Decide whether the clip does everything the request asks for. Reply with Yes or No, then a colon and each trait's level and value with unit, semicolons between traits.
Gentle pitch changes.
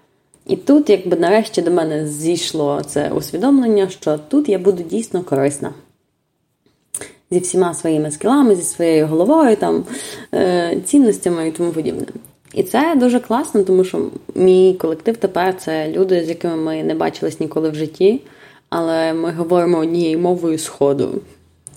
No: average, 3.7 semitones